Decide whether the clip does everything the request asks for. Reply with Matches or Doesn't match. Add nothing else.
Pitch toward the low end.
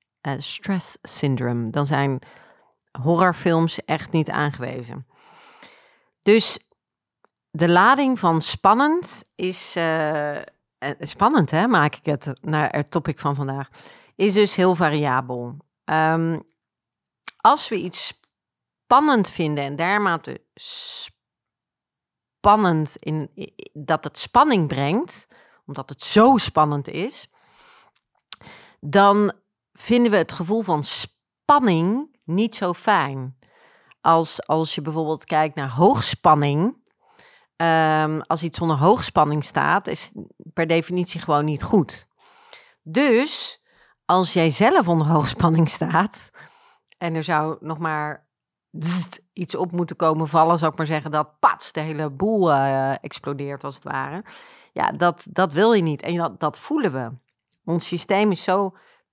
Doesn't match